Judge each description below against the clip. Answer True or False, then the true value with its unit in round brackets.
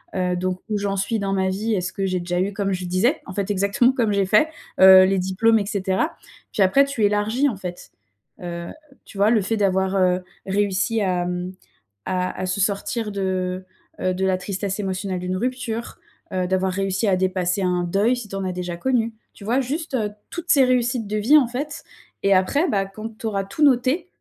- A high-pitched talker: True (195 Hz)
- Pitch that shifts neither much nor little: True (3.3 semitones)